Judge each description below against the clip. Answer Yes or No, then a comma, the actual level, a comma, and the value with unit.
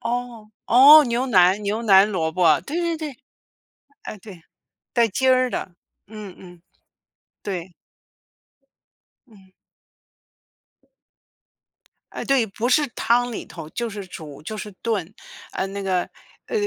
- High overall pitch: Yes, high, 215 Hz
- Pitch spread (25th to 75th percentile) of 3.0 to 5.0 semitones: Yes, average, 4.7 semitones